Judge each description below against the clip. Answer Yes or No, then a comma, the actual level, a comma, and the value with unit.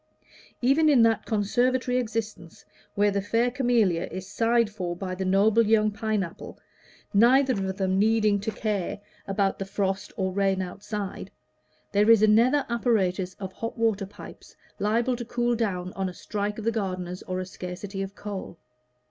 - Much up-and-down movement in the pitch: No, average, 3.1 semitones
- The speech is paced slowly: No, average, 170 wpm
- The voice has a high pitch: Yes, high, 205 Hz